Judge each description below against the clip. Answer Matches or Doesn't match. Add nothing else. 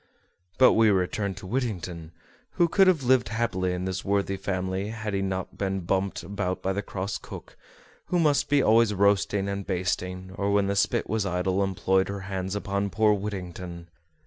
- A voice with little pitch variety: Matches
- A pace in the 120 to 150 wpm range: Doesn't match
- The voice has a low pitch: Matches